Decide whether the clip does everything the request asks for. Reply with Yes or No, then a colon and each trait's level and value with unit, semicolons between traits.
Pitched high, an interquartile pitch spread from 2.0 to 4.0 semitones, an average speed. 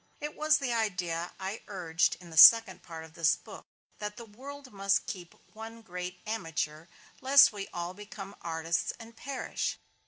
No: high, 195 Hz; average, 4.8 semitones; average, 165 wpm